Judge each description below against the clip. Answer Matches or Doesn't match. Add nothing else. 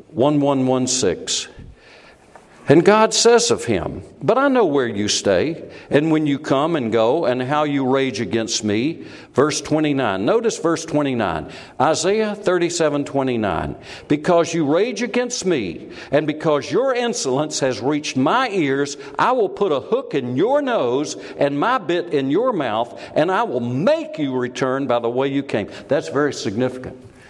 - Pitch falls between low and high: Matches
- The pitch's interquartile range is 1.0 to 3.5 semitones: Doesn't match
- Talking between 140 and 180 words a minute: Matches